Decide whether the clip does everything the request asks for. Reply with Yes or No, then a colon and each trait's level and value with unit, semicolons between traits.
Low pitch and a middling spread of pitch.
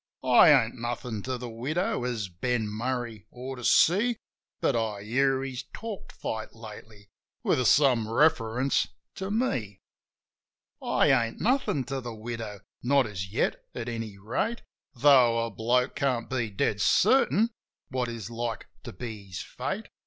Yes: low, 120 Hz; average, 3.3 semitones